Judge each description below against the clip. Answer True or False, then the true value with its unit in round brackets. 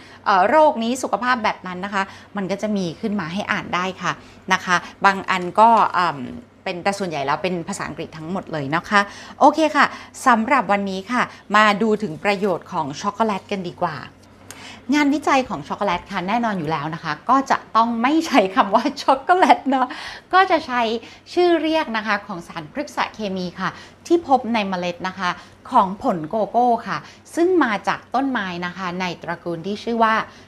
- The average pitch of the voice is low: False (205 Hz)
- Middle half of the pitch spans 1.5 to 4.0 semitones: False (5.2 semitones)